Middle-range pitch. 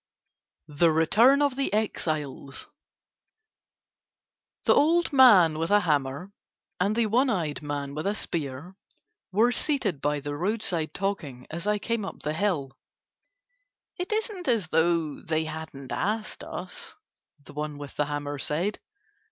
Yes: medium, 170 Hz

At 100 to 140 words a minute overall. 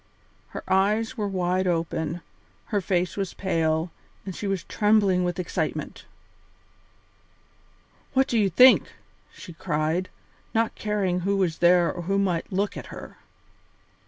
Yes: slow, 135 wpm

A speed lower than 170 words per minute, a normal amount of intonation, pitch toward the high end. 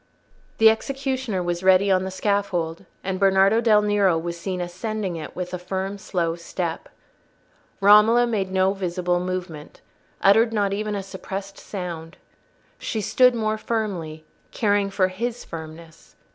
Yes: average, 145 wpm; average, 3.0 semitones; high, 195 Hz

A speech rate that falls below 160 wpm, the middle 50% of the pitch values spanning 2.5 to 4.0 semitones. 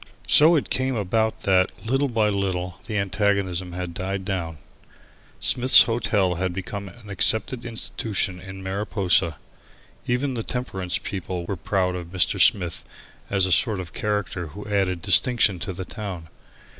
Yes: average, 145 wpm; average, 3.2 semitones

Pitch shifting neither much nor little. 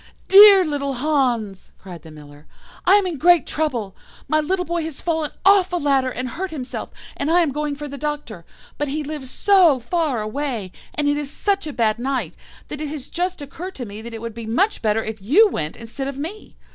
No: wide, 6.0 semitones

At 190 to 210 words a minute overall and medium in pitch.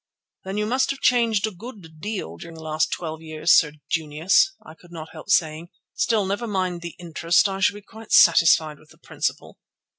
Yes: average, 200 wpm; medium, 175 Hz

